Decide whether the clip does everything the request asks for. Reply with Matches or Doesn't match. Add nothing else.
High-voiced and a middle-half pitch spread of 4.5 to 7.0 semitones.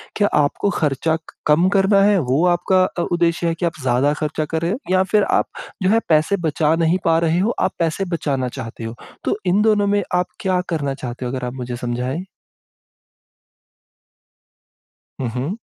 Doesn't match